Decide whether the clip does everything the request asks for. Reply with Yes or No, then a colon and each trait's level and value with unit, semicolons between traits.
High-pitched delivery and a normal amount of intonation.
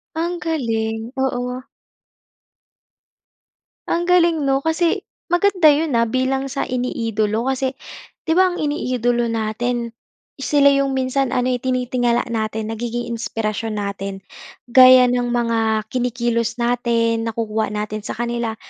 Yes: high, 245 Hz; average, 3.0 semitones